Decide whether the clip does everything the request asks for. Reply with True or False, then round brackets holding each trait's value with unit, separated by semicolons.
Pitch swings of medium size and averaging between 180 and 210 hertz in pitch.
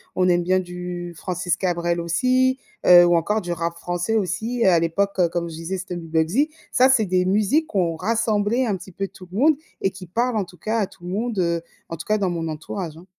True (3.7 semitones; 185 Hz)